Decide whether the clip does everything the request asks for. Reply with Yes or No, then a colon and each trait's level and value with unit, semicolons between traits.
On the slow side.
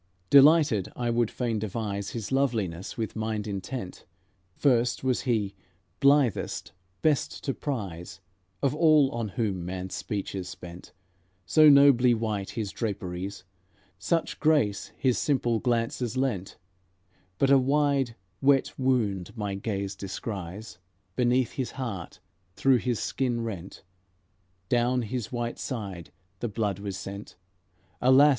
Yes: slow, 125 wpm